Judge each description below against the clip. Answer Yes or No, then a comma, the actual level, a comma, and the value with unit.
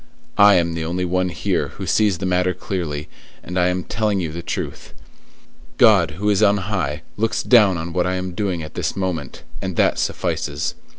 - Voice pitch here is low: Yes, very low, 90 Hz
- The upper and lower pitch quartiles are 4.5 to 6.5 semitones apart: No, average, 2.8 semitones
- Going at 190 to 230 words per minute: Yes, average, 195 wpm